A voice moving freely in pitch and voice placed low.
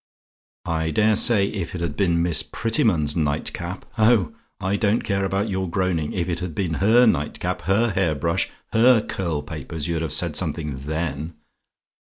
No: average, 4.0 semitones; very low, 85 Hz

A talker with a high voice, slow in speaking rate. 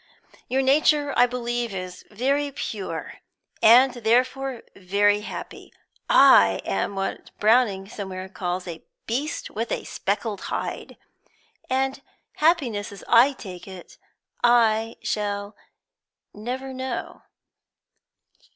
Yes: high, 225 Hz; slow, 105 wpm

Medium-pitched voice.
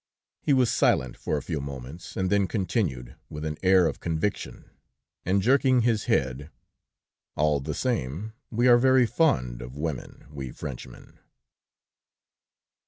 No: very low, 85 Hz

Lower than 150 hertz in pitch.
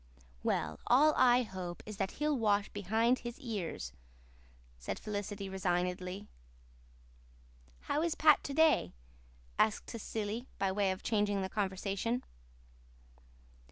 No: high, 205 Hz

